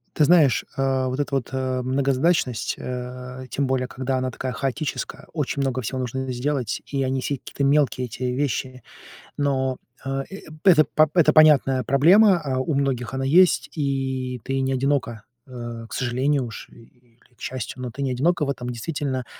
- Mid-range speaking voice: No, low, 130 Hz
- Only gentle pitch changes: Yes, narrow, 1.9 semitones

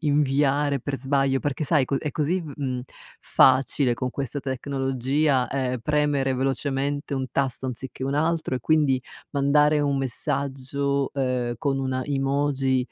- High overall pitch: No, low, 135 Hz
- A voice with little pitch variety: Yes, narrow, 1.6 semitones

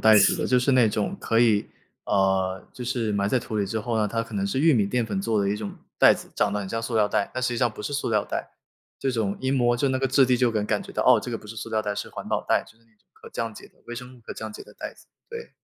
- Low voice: Yes, low, 115 Hz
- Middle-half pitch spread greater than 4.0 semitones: No, average, 3.2 semitones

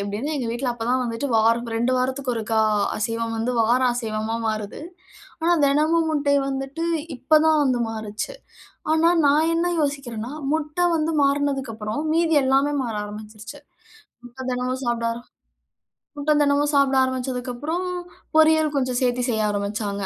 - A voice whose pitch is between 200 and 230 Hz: No, very high, 255 Hz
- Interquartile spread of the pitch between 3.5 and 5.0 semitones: Yes, average, 4.2 semitones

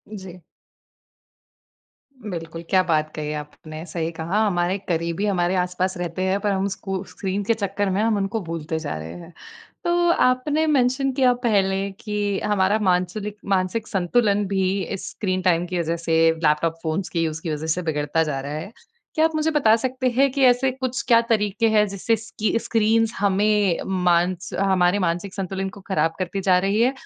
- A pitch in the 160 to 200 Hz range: Yes, high, 190 Hz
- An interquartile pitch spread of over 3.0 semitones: Yes, average, 4.2 semitones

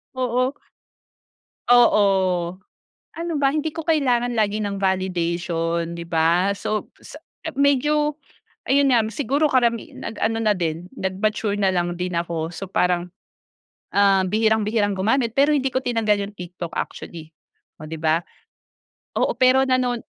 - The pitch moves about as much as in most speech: No, wide, 6.1 semitones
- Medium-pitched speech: No, high, 210 Hz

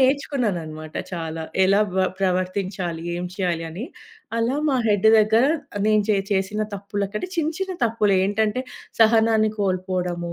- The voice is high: Yes, high, 200 Hz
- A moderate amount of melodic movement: Yes, average, 3.5 semitones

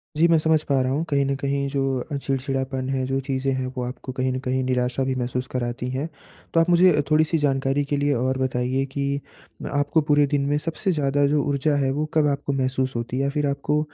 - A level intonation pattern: Yes, narrow, 1.9 semitones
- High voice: No, medium, 140 Hz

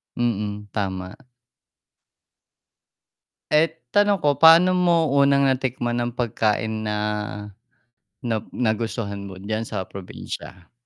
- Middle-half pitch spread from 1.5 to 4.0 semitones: No, average, 5.1 semitones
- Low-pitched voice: Yes, low, 115 Hz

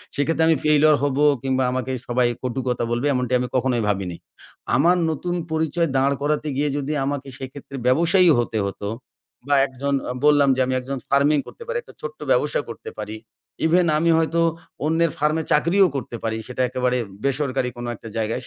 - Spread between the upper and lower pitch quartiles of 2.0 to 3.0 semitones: No, average, 4.0 semitones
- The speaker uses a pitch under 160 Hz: Yes, medium, 140 Hz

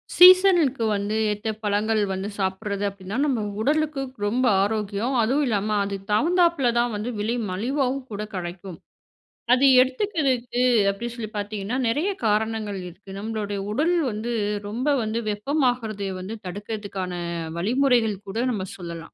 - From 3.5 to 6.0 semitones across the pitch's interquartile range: Yes, average, 4.1 semitones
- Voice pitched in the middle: No, high, 220 Hz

